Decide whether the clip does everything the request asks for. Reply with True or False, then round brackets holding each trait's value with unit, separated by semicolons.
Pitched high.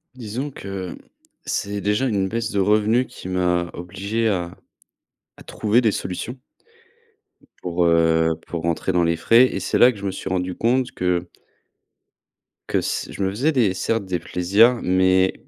False (95 Hz)